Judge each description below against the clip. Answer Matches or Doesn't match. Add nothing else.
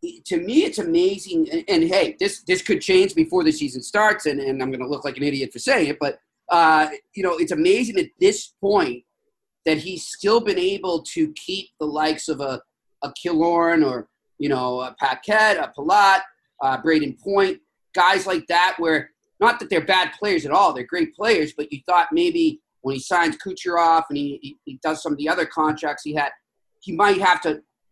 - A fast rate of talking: Matches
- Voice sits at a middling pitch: Matches